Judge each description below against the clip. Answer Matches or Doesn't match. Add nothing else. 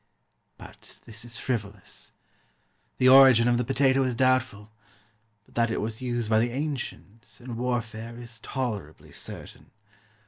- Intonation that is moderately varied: Doesn't match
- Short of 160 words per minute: Matches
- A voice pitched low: Matches